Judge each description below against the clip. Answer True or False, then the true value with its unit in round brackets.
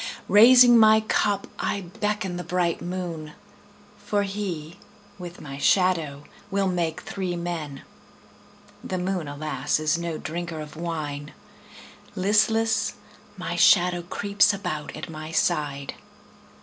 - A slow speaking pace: True (120 wpm)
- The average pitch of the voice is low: False (175 Hz)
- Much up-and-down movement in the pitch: False (4.4 semitones)